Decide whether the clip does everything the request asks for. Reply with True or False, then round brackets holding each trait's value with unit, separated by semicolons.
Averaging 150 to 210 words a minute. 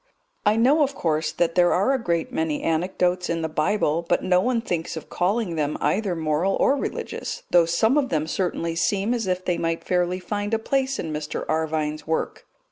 True (205 wpm)